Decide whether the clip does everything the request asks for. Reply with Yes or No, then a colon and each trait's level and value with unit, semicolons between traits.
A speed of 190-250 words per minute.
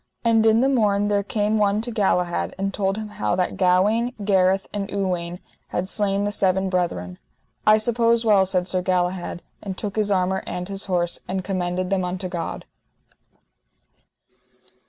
No: average, 165 wpm